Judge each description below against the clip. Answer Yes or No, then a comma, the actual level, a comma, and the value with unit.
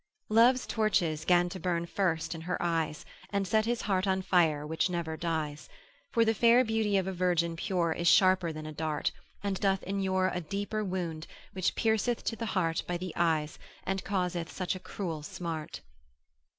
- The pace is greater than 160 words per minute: Yes, average, 185 wpm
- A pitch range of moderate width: Yes, average, 3.3 semitones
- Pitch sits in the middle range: Yes, medium, 180 Hz